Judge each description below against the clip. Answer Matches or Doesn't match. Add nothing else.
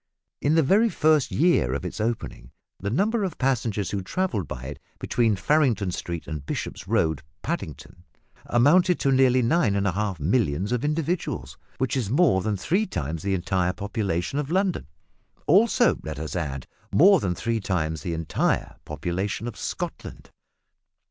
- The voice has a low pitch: Matches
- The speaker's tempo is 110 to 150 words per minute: Doesn't match